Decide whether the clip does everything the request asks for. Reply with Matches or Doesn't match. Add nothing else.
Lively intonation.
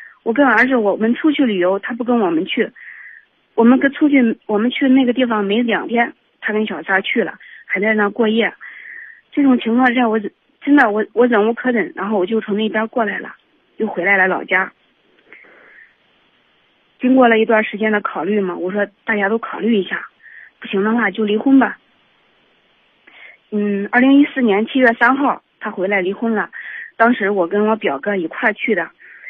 Doesn't match